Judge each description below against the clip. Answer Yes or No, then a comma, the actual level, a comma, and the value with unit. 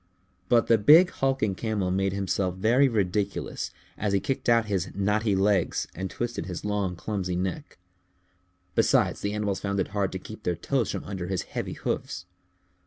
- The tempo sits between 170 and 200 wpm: Yes, average, 175 wpm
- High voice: No, low, 100 Hz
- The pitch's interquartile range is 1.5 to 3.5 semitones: Yes, average, 2.7 semitones